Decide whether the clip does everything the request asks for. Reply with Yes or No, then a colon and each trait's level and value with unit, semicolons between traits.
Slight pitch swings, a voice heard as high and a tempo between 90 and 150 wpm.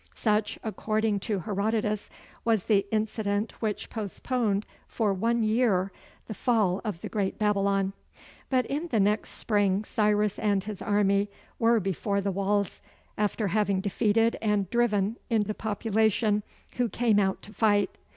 Yes: narrow, 1.8 semitones; high, 210 Hz; average, 145 wpm